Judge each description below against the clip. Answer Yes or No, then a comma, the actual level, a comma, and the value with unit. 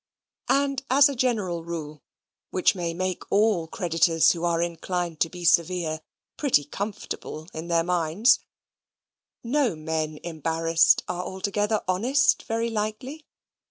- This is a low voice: No, medium, 180 Hz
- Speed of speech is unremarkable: No, slow, 125 wpm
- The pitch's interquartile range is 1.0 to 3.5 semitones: No, average, 4.9 semitones